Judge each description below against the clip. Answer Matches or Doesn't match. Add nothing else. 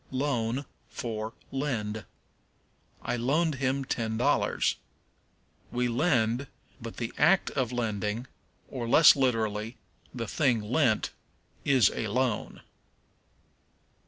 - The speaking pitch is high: Doesn't match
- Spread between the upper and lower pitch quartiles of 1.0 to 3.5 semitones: Matches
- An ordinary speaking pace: Doesn't match